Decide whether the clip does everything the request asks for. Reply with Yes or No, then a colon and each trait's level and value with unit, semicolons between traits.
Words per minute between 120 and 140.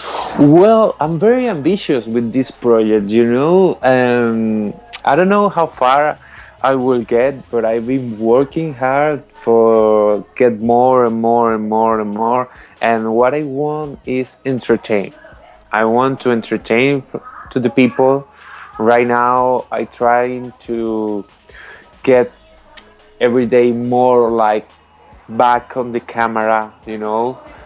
Yes: slow, 135 wpm